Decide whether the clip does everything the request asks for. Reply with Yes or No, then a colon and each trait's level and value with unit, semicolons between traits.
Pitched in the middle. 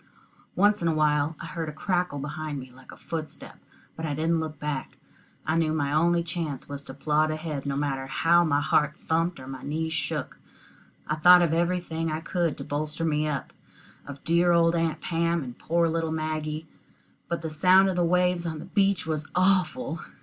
Yes: medium, 160 Hz